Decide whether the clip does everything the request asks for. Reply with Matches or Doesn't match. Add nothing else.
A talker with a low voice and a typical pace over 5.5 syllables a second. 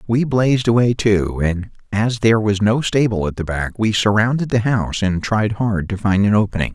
Doesn't match